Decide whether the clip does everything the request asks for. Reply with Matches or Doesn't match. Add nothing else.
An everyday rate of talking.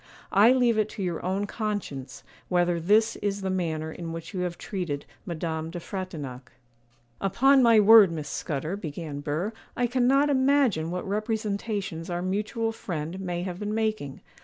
Matches